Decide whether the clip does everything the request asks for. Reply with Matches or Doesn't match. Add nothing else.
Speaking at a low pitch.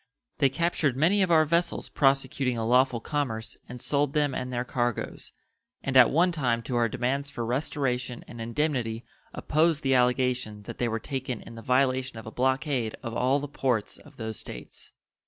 Matches